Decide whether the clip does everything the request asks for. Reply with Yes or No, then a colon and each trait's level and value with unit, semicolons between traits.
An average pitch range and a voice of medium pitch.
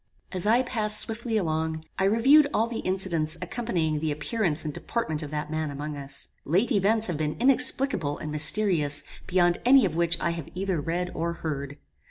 No: wide, 5.7 semitones; medium, 170 Hz